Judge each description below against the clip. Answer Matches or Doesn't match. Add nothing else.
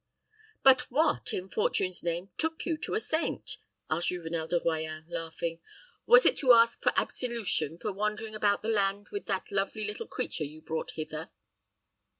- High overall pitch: Matches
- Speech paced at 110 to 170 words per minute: Matches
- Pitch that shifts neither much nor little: Doesn't match